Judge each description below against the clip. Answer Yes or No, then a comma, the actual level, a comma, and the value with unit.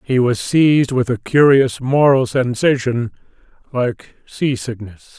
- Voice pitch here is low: Yes, low, 125 Hz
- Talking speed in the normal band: No, slow, 115 wpm